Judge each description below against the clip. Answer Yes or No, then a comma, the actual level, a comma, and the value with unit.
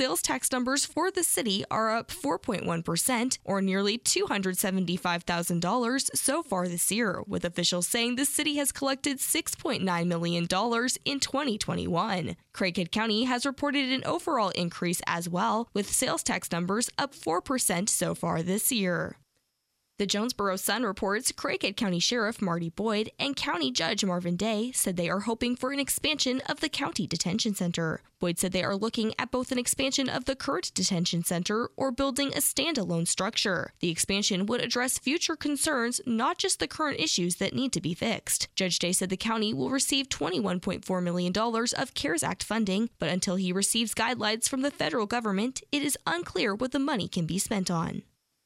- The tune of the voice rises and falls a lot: Yes, wide, 6.0 semitones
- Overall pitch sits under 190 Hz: No, high, 220 Hz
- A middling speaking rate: Yes, average, 170 wpm